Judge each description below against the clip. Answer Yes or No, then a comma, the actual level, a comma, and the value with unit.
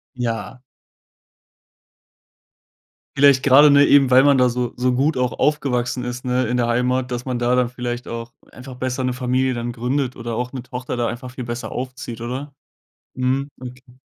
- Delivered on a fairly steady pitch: Yes, narrow, 1.3 semitones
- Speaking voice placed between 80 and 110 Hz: No, low, 125 Hz